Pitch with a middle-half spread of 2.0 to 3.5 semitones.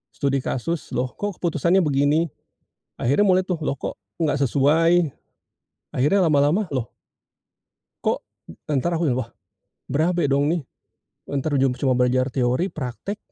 No: average, 4.4 semitones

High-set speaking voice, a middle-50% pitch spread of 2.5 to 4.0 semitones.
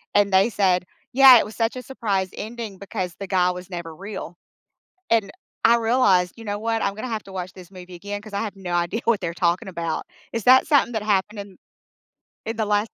Yes: high, 200 Hz; average, 3.6 semitones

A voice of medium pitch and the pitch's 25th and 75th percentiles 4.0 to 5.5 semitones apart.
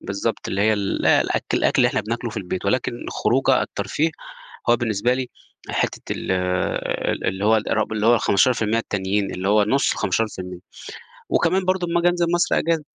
No: low, 110 Hz; average, 4.6 semitones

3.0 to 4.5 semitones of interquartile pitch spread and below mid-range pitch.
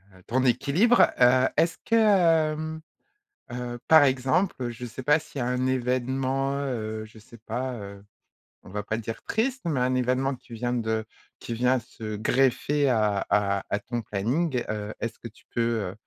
Yes: average, 3.6 semitones; low, 125 Hz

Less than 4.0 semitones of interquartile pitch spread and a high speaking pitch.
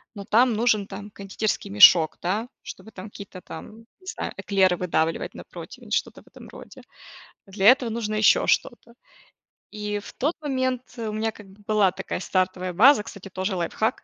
Yes: average, 2.9 semitones; high, 210 Hz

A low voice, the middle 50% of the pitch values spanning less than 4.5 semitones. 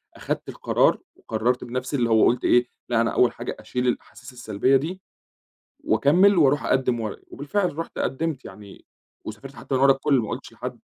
Yes: low, 130 Hz; average, 3.2 semitones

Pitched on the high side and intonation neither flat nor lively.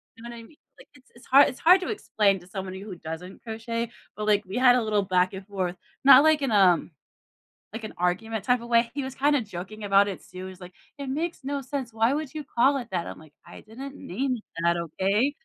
No: high, 225 Hz; wide, 5.8 semitones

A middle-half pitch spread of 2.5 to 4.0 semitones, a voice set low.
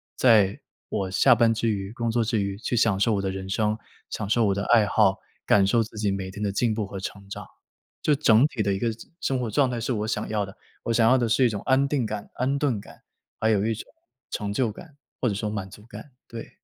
Yes: average, 2.9 semitones; low, 110 Hz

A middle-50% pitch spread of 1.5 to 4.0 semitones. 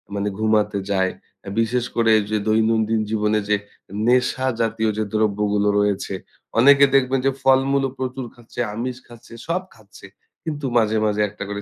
Yes: average, 3.3 semitones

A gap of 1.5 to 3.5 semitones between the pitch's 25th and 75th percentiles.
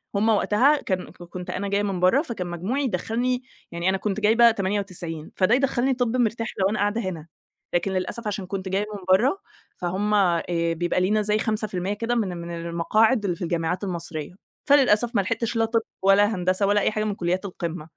No: average, 3.9 semitones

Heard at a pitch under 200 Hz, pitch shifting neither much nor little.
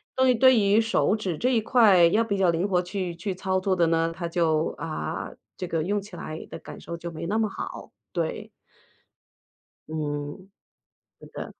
Yes: medium, 185 Hz; average, 3.9 semitones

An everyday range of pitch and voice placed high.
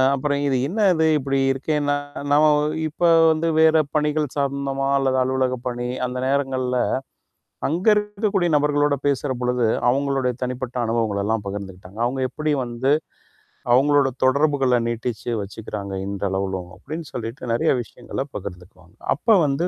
No: average, 3.8 semitones; low, 135 Hz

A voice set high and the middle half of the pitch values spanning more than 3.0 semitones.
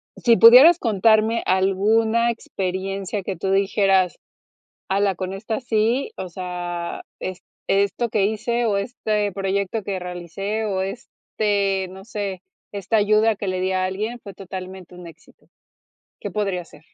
No: high, 195 Hz; narrow, 2.6 semitones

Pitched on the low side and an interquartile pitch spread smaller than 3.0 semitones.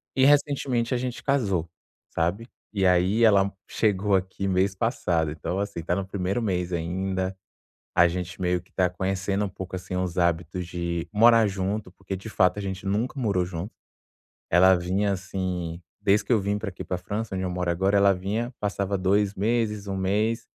Yes: very low, 95 Hz; narrow, 2.4 semitones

